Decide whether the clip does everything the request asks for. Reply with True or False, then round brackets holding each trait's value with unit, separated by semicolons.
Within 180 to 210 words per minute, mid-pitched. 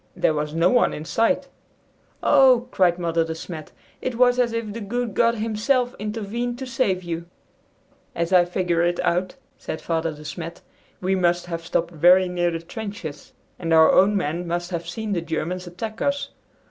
True (185 wpm; 180 Hz)